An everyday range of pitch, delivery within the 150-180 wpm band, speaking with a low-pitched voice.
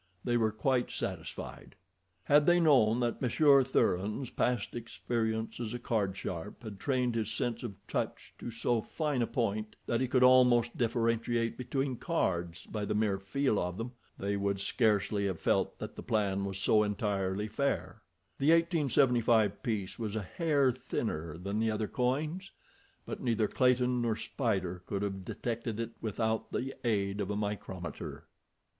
Yes: average, 3.6 semitones; average, 165 wpm; low, 115 Hz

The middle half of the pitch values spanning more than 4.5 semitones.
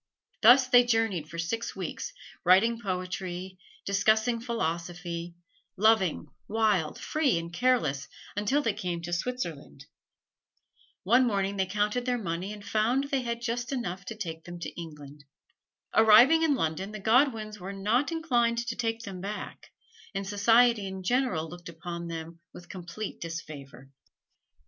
Yes: average, 5.2 semitones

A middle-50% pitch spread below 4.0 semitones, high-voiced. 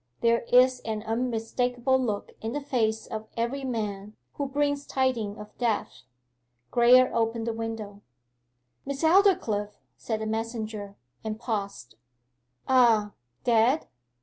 Yes: average, 2.8 semitones; high, 230 Hz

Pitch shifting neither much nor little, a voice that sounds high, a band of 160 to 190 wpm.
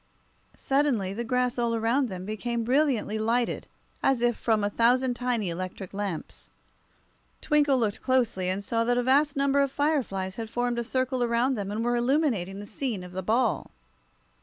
Yes: average, 4.0 semitones; high, 235 Hz; average, 175 wpm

